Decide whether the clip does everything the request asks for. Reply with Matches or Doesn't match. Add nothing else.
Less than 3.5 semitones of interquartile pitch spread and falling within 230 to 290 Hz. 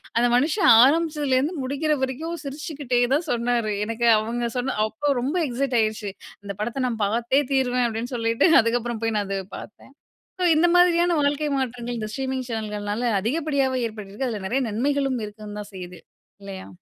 Doesn't match